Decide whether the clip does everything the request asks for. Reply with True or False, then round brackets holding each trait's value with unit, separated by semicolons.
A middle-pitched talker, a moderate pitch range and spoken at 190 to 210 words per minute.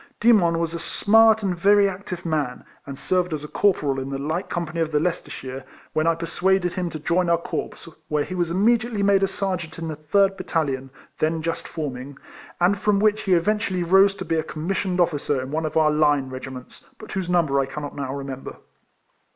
True (170 Hz; 4.3 semitones; 200 wpm)